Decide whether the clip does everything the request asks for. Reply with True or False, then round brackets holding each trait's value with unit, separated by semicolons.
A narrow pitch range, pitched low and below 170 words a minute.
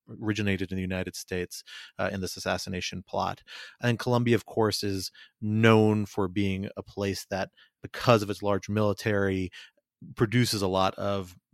True (2.2 semitones; 100 Hz; 155 wpm)